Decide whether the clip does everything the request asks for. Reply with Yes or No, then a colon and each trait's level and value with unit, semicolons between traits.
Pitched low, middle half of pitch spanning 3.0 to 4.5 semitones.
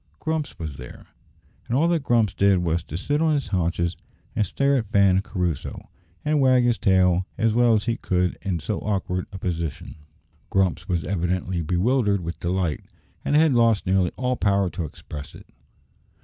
No: very low, 95 Hz; average, 5.3 semitones